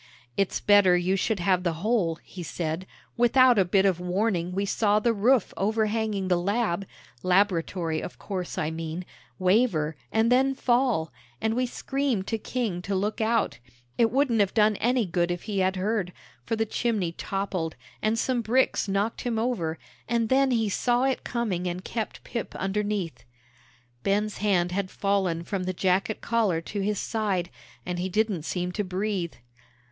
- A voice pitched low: No, high, 200 Hz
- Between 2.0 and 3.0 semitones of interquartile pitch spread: No, average, 3.9 semitones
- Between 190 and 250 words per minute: No, average, 170 wpm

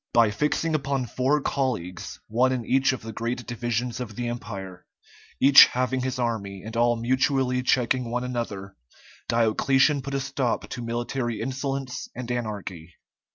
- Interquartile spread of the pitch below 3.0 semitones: Yes, narrow, 2.4 semitones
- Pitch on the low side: Yes, low, 120 Hz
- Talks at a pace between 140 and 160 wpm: Yes, average, 155 wpm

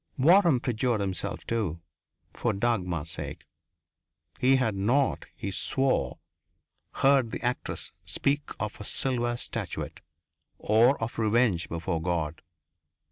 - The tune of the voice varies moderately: No, wide, 5.7 semitones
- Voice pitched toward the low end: Yes, low, 115 Hz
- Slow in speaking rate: Yes, slow, 115 wpm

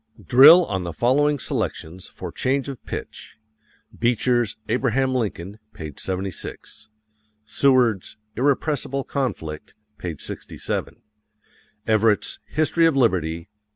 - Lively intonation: Yes, wide, 6.3 semitones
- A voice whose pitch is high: No, low, 120 Hz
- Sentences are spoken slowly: Yes, slow, 105 wpm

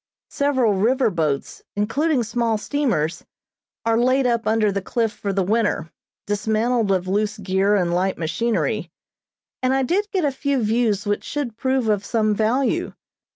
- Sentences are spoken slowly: No, average, 155 wpm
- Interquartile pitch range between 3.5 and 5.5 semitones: Yes, average, 4.1 semitones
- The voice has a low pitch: No, high, 220 Hz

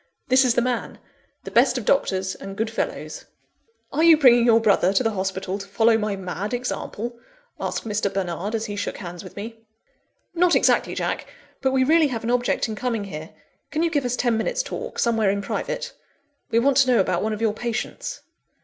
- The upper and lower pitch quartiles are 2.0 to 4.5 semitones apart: Yes, average, 4.0 semitones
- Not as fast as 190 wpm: No, fast, 205 wpm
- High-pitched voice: Yes, high, 225 Hz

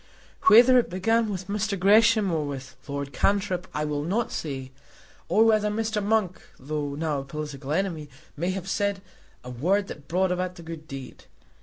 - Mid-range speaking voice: Yes, medium, 180 Hz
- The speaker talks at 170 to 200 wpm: Yes, average, 175 wpm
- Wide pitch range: Yes, wide, 5.7 semitones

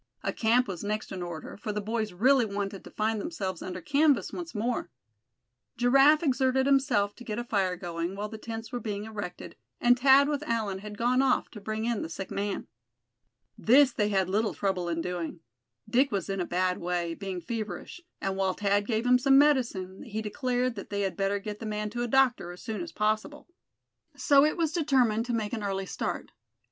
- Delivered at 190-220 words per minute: Yes, fast, 205 wpm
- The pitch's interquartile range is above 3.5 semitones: Yes, average, 4.4 semitones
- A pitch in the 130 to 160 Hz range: No, high, 215 Hz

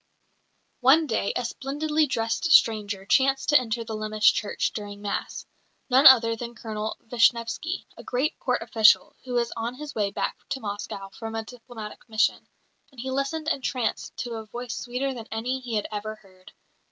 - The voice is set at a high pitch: Yes, high, 235 Hz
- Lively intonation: No, average, 3.3 semitones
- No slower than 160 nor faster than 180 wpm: Yes, average, 175 wpm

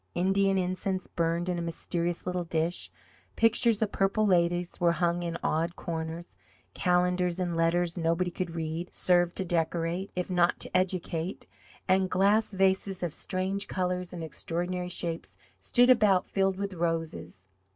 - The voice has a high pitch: No, medium, 180 Hz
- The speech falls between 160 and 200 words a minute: No, average, 150 wpm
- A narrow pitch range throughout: Yes, narrow, 1.9 semitones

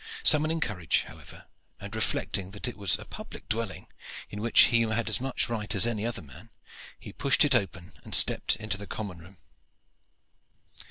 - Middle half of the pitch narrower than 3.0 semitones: No, average, 3.3 semitones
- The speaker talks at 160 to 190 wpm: Yes, average, 175 wpm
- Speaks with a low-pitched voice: Yes, low, 110 Hz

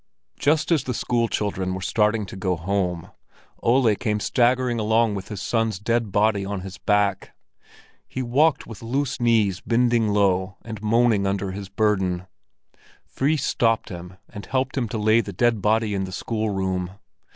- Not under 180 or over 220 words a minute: No, average, 165 wpm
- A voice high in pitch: No, low, 105 Hz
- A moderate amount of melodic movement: Yes, average, 3.4 semitones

